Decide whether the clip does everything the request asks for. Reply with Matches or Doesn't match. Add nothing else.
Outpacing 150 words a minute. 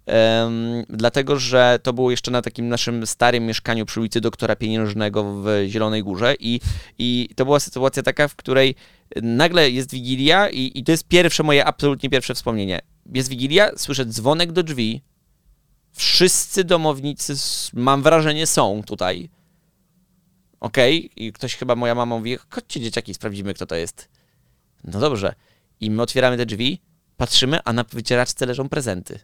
Matches